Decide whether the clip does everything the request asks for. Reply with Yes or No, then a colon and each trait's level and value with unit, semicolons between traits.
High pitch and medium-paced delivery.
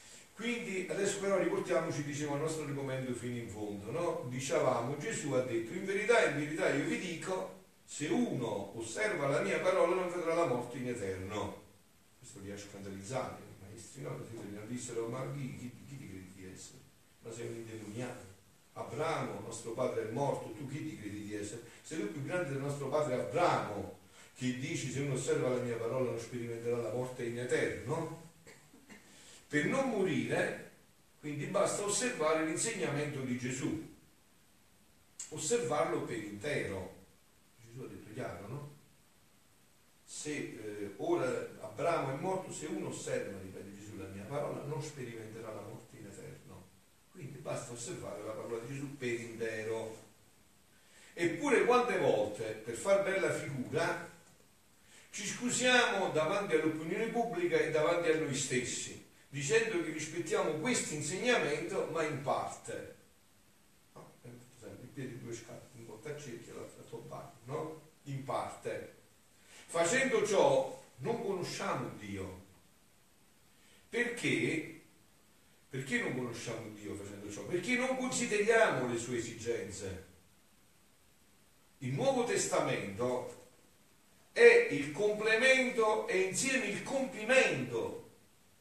No: medium, 140 Hz; average, 135 wpm